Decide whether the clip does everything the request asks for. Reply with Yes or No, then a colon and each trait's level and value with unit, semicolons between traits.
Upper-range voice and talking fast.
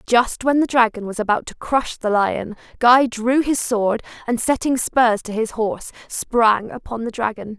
No: high, 235 Hz; average, 190 wpm